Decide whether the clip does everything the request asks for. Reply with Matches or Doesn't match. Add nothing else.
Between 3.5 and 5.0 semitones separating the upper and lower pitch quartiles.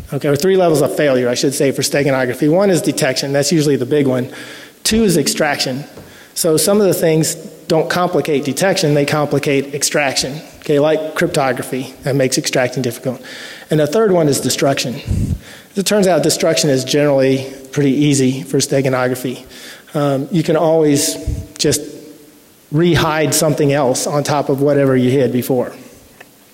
Doesn't match